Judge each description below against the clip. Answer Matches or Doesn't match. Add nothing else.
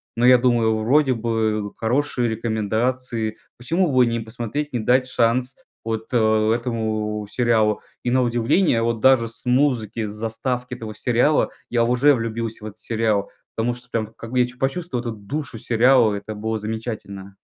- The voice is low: Matches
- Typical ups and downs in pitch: Doesn't match